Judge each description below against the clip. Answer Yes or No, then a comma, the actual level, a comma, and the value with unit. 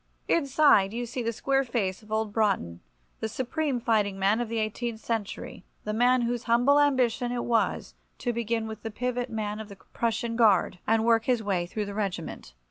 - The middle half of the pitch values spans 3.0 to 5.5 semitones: No, narrow, 2.5 semitones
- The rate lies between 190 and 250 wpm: Yes, average, 195 wpm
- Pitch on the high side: Yes, high, 225 Hz